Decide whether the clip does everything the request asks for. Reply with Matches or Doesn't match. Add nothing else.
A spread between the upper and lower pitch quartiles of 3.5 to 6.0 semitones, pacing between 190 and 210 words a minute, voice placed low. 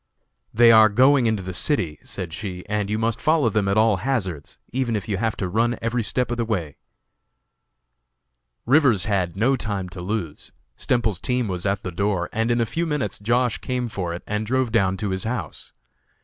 Matches